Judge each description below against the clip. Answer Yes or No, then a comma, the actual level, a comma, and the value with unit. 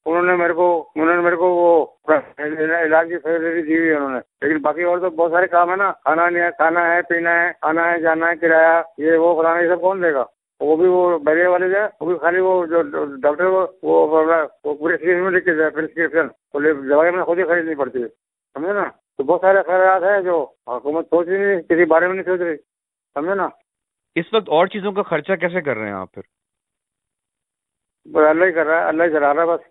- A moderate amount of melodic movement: No, narrow, 2.1 semitones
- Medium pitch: Yes, medium, 170 Hz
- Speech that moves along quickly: Yes, fast, 205 wpm